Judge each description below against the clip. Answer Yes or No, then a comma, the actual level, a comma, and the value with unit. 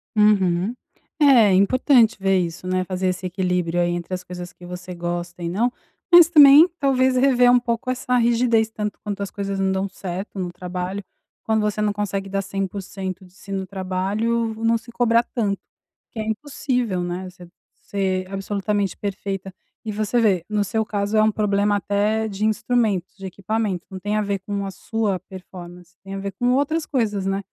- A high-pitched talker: Yes, high, 200 Hz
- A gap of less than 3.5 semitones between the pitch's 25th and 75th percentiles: Yes, average, 3.1 semitones